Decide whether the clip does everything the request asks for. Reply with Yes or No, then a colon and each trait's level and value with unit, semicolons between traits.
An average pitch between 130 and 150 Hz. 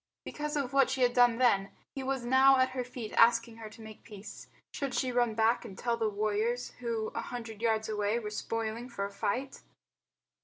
No: high, 230 Hz